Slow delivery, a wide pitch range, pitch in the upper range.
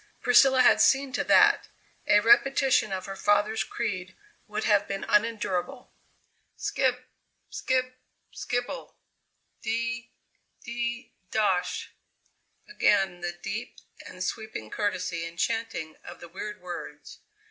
No: slow, 115 wpm; average, 4.6 semitones; high, 220 Hz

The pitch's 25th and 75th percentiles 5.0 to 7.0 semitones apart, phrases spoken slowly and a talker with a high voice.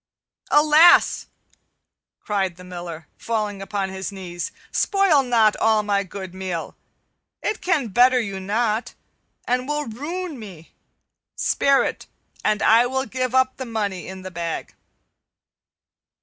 Yes: wide, 5.5 semitones; slow, 130 wpm; high, 215 Hz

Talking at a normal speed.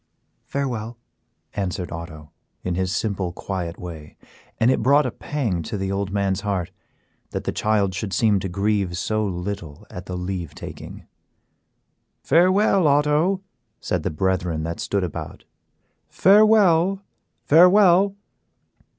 No: slow, 130 wpm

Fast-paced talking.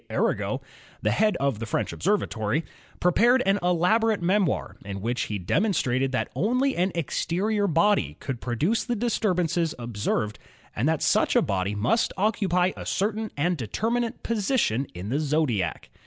No: average, 155 wpm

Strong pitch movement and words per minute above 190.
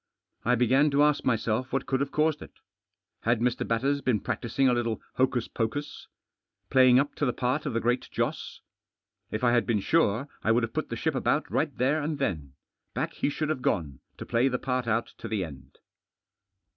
No: average, 3.4 semitones; fast, 205 wpm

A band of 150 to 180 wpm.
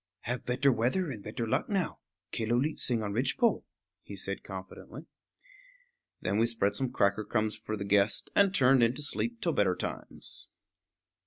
Yes: average, 165 wpm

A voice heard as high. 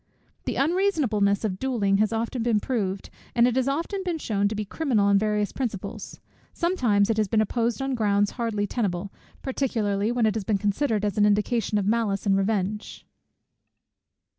Yes: high, 215 Hz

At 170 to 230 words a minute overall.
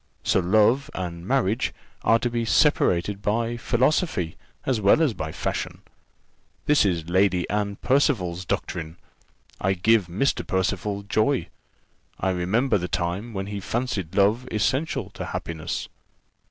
No: slow, 135 wpm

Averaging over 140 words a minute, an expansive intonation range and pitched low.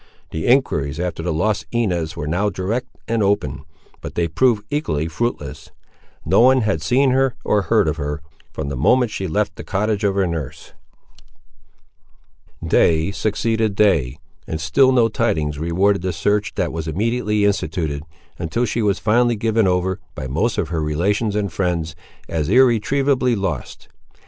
Yes: average, 165 wpm; wide, 6.0 semitones; low, 100 Hz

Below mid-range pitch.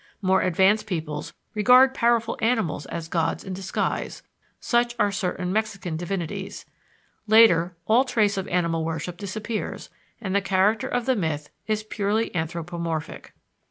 No: high, 195 Hz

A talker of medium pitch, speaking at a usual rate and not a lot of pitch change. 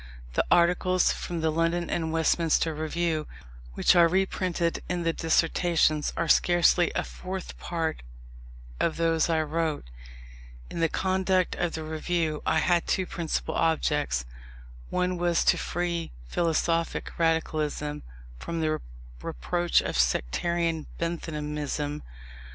No: medium, 165 Hz; slow, 120 wpm; narrow, 1.8 semitones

